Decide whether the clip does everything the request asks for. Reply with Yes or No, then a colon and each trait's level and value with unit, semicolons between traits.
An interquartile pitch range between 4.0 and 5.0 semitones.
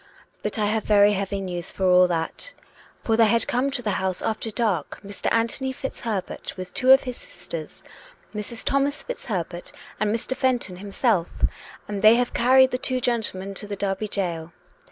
Yes: average, 4.4 semitones